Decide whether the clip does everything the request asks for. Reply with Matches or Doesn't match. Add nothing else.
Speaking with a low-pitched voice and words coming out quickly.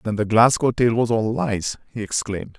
Matches